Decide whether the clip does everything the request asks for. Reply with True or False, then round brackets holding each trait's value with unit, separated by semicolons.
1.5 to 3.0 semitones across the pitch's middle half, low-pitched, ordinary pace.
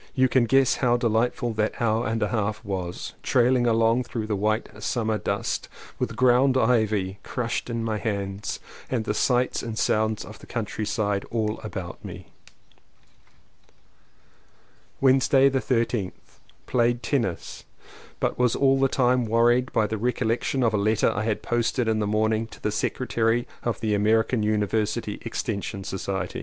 True (2.4 semitones; 115 Hz; 160 wpm)